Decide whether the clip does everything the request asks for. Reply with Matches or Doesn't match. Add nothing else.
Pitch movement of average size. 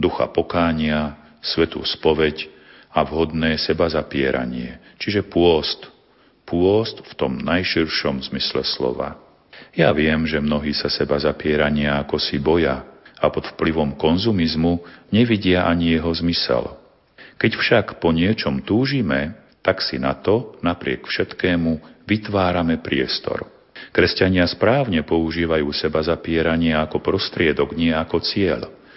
Doesn't match